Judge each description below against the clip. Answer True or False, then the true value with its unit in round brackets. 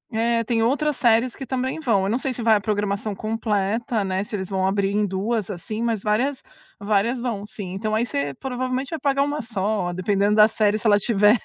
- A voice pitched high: True (215 Hz)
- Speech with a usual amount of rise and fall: True (3.1 semitones)